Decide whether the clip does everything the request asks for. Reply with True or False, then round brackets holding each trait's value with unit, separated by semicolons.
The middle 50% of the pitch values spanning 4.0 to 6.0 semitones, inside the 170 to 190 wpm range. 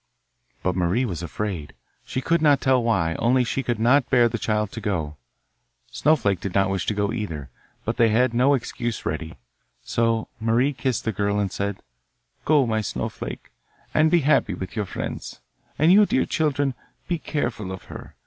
True (5.1 semitones; 180 wpm)